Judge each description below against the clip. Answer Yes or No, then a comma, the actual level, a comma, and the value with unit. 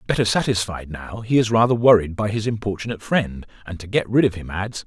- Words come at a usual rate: No, fast, 220 wpm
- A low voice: Yes, low, 105 Hz